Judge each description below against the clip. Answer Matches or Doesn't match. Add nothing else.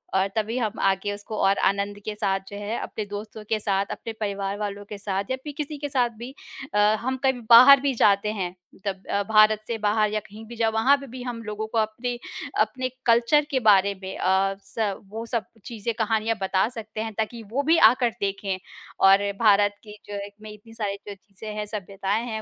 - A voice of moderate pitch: Doesn't match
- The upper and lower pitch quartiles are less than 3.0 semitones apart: Matches